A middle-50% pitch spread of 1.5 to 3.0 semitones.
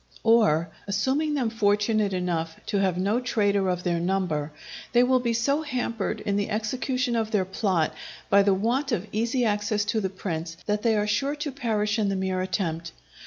No: average, 3.8 semitones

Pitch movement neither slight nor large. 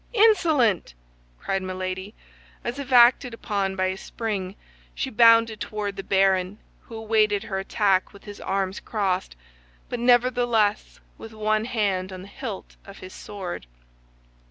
Yes: average, 3.1 semitones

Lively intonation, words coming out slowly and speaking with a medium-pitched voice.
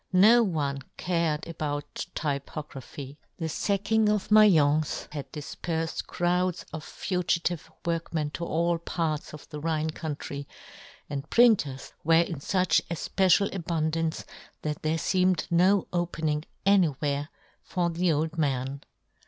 No: average, 3.0 semitones; slow, 125 wpm; medium, 160 Hz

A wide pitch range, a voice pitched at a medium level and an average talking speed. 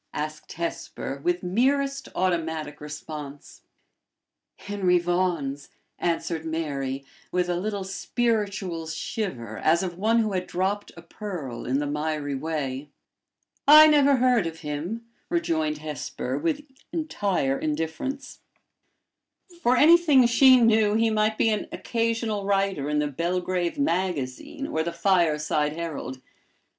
No: wide, 6.4 semitones; medium, 175 Hz; slow, 125 wpm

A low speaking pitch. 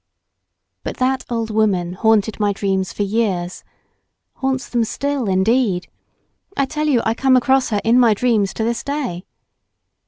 No: high, 225 Hz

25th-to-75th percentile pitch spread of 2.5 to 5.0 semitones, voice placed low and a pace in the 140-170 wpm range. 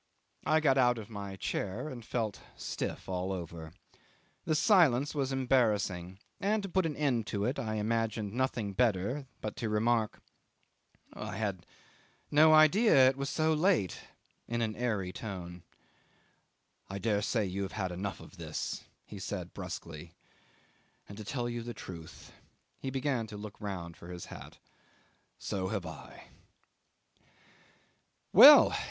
No: wide, 5.5 semitones; low, 110 Hz; average, 145 wpm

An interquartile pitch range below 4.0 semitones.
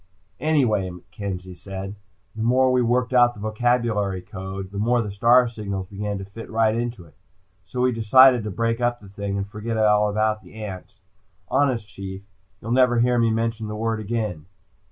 Yes: average, 3.3 semitones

